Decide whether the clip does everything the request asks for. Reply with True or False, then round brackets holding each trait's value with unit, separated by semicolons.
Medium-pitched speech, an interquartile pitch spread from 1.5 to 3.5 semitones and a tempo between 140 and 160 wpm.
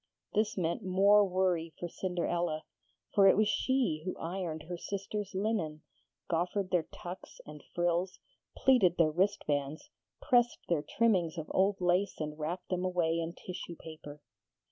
True (180 Hz; 3.2 semitones; 145 wpm)